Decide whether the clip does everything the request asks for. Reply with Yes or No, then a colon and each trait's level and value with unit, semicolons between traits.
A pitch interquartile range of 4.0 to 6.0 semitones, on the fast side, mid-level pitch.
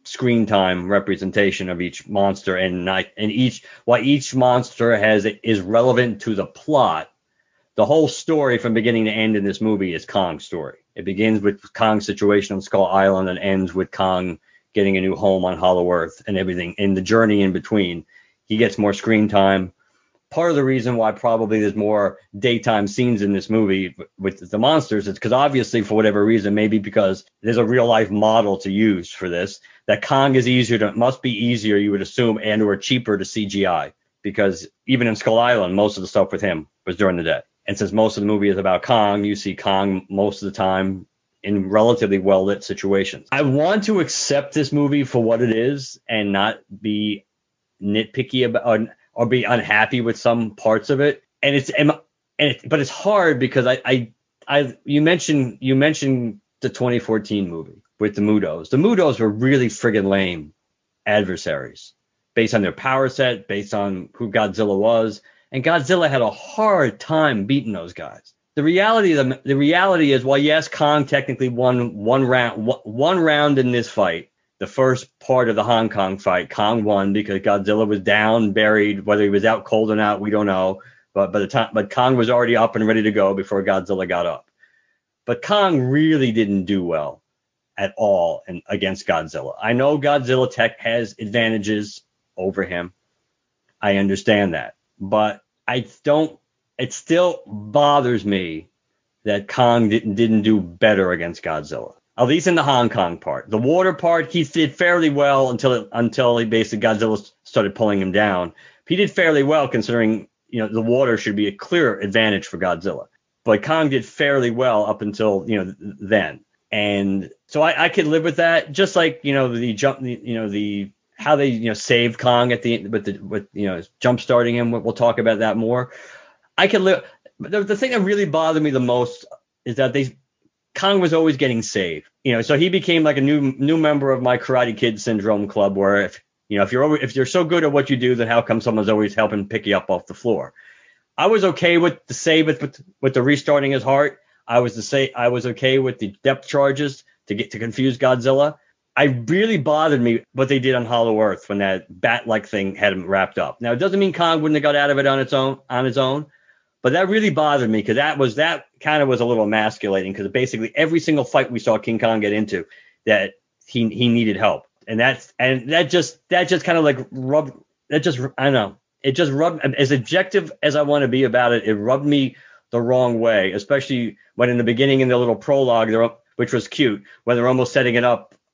No: average, 4.8 semitones; fast, 210 wpm; low, 115 Hz